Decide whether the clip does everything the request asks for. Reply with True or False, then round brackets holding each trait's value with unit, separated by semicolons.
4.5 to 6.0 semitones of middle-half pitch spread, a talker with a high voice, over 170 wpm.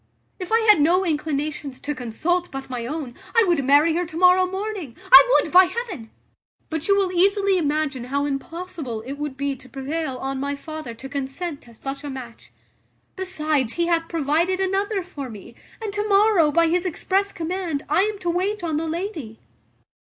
True (5.0 semitones; 320 Hz; 190 wpm)